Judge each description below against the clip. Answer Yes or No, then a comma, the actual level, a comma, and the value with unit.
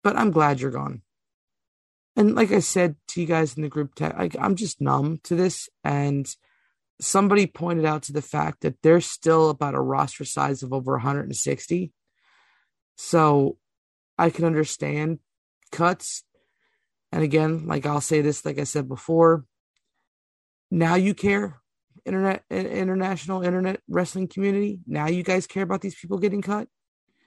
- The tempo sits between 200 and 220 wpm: No, average, 155 wpm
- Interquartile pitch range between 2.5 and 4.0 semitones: No, average, 4.8 semitones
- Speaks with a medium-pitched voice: Yes, medium, 160 Hz